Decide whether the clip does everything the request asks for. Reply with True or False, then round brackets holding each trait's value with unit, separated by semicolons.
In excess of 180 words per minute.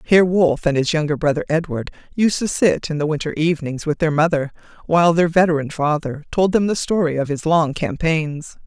True (200 wpm)